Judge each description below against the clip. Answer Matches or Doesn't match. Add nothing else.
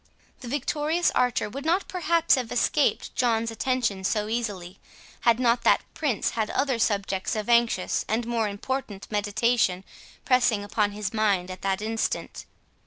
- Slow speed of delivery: Doesn't match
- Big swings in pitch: Doesn't match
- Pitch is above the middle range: Matches